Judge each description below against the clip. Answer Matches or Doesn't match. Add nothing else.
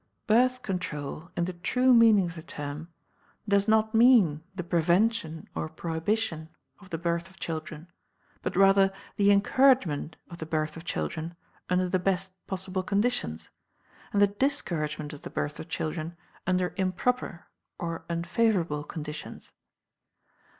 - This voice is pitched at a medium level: Matches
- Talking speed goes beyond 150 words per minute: Doesn't match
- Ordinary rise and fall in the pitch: Matches